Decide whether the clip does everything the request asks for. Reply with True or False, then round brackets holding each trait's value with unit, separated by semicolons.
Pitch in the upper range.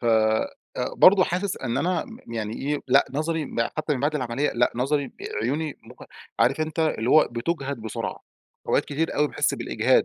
False (140 Hz)